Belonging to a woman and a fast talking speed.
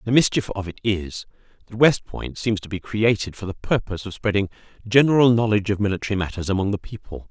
No: male; fast, 215 wpm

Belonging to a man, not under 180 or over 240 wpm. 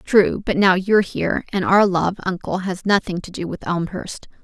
No: female; fast, 205 wpm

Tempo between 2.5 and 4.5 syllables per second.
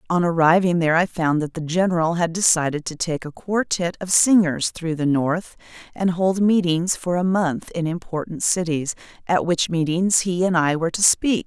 No: 5.0 syllables/s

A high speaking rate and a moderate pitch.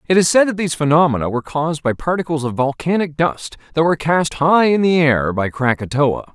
Yes: fast, 210 wpm; medium, 150 Hz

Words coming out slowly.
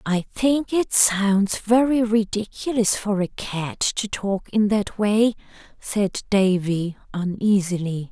Yes: slow, 125 wpm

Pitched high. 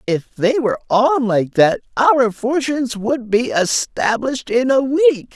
Yes: high, 245 Hz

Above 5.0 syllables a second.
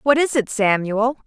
No: 4.6 syllables/s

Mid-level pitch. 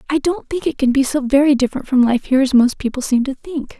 No: very high, 270 Hz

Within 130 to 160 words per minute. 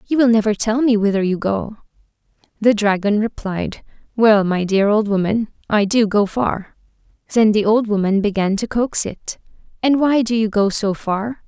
No: average, 185 wpm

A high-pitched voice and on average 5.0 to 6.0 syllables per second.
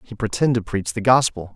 No: low, 110 Hz; 5.5 syllables/s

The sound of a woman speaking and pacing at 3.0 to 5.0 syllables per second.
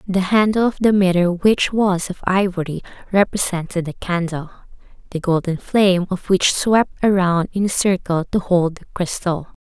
Yes: female; 4.7 syllables/s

